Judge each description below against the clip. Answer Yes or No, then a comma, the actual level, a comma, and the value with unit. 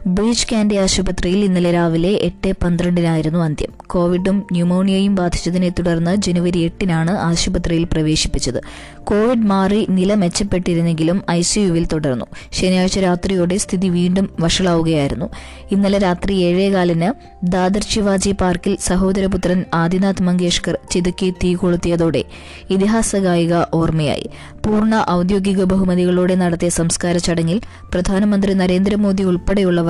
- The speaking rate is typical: Yes, average, 100 wpm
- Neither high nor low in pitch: Yes, medium, 180 Hz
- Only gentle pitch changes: Yes, narrow, 2.1 semitones